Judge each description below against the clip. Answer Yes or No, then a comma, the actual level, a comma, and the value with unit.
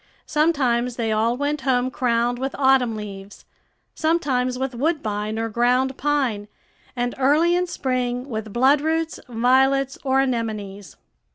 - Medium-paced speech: No, slow, 125 wpm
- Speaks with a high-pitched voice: Yes, very high, 250 Hz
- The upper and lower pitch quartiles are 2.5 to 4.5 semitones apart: Yes, average, 2.9 semitones